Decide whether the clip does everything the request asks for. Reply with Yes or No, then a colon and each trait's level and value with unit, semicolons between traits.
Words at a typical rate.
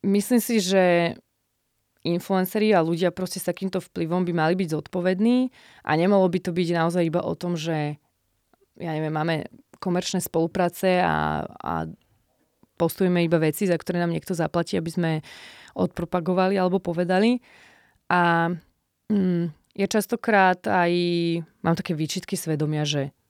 Yes: average, 140 wpm